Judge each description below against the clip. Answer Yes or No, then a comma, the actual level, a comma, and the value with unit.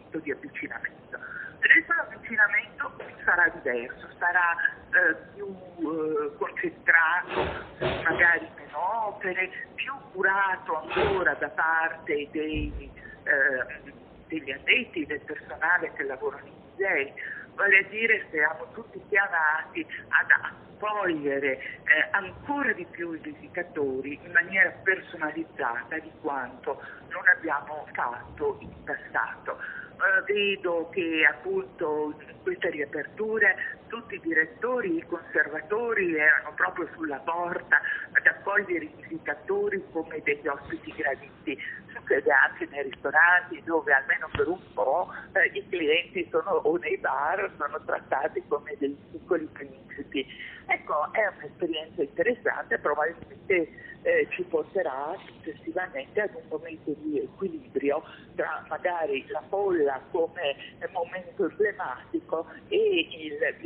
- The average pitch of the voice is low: No, high, 195 Hz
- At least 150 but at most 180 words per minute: No, slow, 115 wpm